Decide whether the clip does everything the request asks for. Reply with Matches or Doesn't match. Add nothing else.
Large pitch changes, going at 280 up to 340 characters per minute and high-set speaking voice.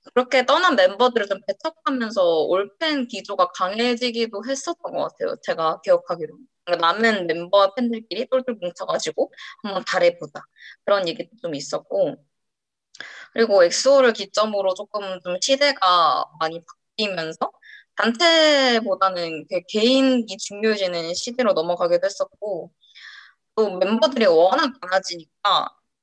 Matches